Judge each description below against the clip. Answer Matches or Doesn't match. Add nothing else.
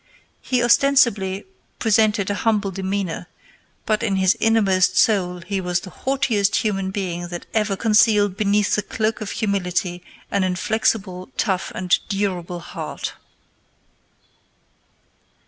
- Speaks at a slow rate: Matches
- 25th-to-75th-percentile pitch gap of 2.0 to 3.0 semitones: Matches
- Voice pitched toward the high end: Matches